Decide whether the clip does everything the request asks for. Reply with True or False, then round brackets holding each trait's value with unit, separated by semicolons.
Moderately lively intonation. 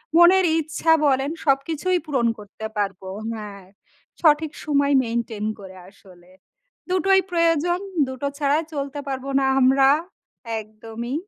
False (6.1 semitones)